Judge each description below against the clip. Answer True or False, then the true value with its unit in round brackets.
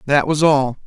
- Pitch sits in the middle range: True (145 Hz)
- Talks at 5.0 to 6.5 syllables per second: False (4.7 syllables/s)